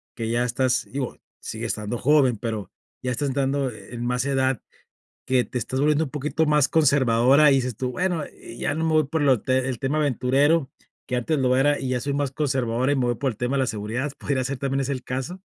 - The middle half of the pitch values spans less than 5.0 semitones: Yes, narrow, 2.5 semitones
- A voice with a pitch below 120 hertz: No, low, 130 Hz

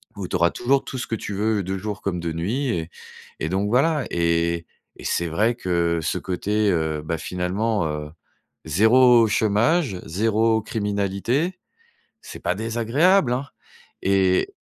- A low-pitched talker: Yes, low, 105 Hz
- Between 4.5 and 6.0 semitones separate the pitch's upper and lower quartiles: Yes, average, 5.0 semitones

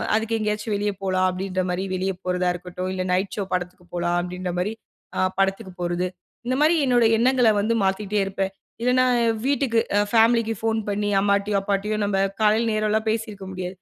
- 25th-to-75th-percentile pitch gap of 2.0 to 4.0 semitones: Yes, average, 3.2 semitones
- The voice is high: Yes, high, 200 Hz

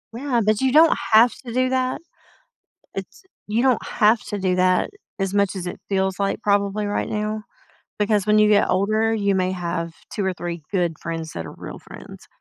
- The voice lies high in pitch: Yes, high, 205 Hz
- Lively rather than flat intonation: No, average, 2.9 semitones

